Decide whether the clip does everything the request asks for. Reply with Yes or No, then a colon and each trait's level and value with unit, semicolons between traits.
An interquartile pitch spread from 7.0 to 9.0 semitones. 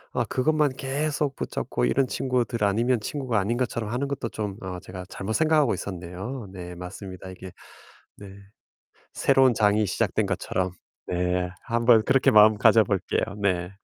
No: wide, 5.6 semitones